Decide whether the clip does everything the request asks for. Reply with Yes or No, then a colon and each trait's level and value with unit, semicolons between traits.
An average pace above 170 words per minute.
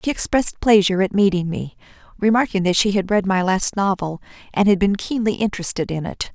Yes: average, 200 wpm